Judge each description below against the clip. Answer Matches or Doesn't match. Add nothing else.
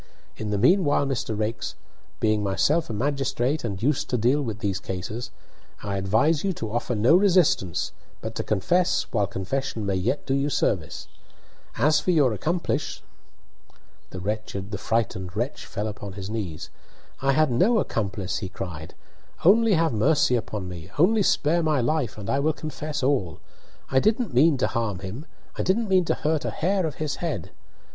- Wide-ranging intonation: Matches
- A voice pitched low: Matches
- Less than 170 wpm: Doesn't match